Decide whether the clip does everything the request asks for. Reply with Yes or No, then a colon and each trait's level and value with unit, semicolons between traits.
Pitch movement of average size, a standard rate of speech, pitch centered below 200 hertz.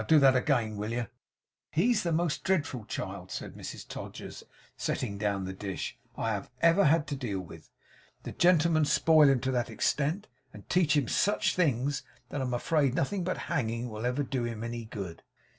No: wide, 5.8 semitones; average, 180 wpm; low, 135 Hz